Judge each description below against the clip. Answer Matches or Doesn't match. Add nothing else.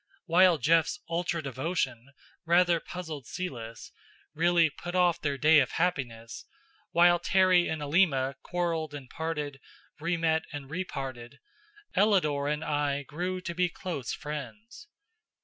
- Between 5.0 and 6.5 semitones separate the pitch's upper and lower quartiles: Doesn't match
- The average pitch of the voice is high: Doesn't match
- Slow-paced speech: Matches